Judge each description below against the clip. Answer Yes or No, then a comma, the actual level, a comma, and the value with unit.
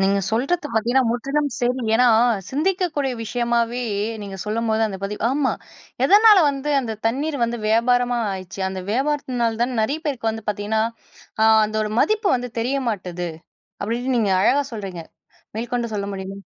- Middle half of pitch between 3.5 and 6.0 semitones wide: Yes, average, 3.9 semitones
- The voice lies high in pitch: Yes, high, 235 Hz